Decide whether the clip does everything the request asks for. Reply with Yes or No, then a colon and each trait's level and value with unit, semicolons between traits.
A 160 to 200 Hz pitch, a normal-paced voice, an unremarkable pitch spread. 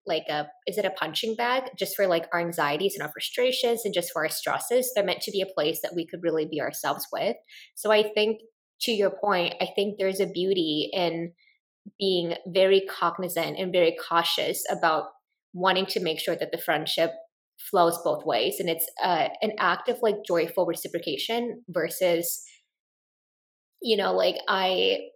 Yes: high, 190 Hz; average, 180 wpm; average, 4.1 semitones